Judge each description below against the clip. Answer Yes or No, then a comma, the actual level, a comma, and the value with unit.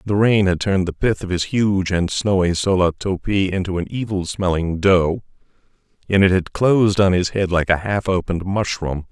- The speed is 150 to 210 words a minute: Yes, average, 200 wpm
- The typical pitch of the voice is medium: No, very low, 95 Hz